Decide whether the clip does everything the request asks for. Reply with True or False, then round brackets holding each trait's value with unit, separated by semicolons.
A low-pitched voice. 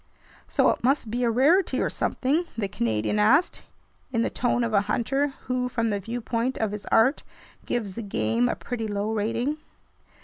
False (230 Hz)